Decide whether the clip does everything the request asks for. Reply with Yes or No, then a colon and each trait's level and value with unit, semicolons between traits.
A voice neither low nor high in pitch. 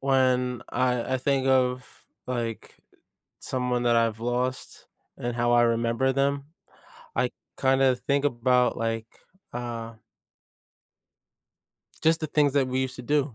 No: low, 125 Hz